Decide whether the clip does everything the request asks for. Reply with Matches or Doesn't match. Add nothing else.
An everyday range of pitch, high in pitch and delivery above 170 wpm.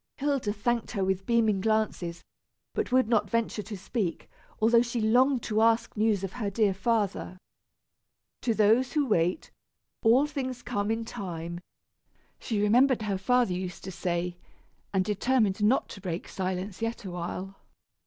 Doesn't match